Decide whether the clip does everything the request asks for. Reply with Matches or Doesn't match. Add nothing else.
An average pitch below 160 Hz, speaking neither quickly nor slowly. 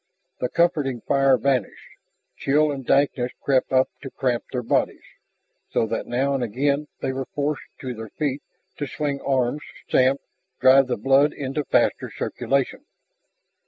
Matches